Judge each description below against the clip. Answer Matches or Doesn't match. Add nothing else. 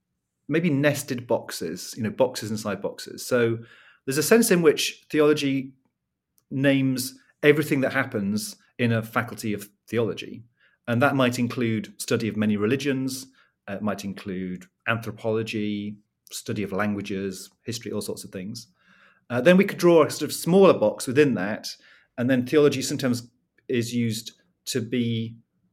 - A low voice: Matches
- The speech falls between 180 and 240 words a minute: Doesn't match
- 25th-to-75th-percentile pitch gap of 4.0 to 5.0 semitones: Matches